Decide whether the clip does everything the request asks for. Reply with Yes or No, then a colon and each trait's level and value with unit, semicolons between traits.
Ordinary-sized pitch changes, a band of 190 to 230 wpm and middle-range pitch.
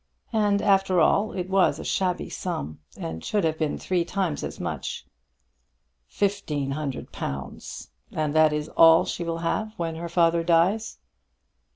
No: average, 3.7 semitones; average, 155 wpm; medium, 170 Hz